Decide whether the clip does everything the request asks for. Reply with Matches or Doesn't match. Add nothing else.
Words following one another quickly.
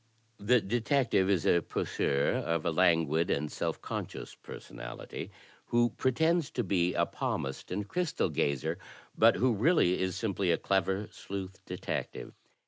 Doesn't match